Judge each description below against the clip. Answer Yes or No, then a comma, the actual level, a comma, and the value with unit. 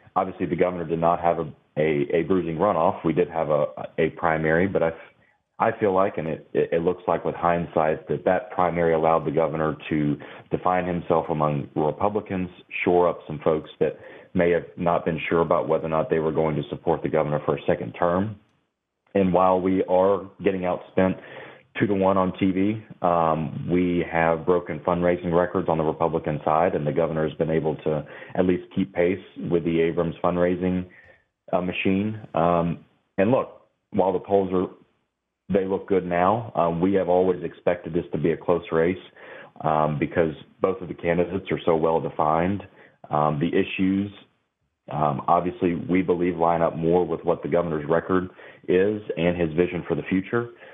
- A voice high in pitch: No, very low, 85 Hz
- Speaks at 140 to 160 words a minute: No, average, 185 wpm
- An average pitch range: No, narrow, 2.2 semitones